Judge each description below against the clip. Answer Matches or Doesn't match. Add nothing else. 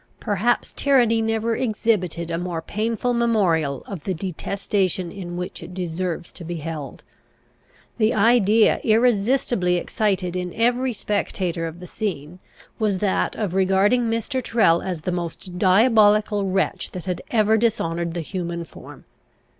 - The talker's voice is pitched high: Matches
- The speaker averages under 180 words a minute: Matches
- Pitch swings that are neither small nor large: Matches